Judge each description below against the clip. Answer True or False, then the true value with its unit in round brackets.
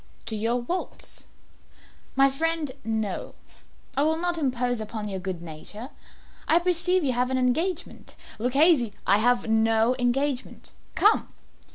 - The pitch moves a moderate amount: False (6.0 semitones)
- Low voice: False (250 Hz)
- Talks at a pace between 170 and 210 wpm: False (140 wpm)